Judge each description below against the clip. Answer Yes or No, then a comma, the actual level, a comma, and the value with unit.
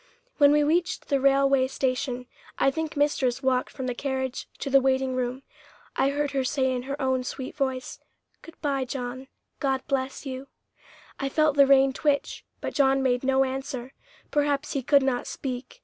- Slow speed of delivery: No, average, 180 wpm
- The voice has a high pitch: Yes, very high, 270 Hz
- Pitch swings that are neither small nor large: No, narrow, 1.3 semitones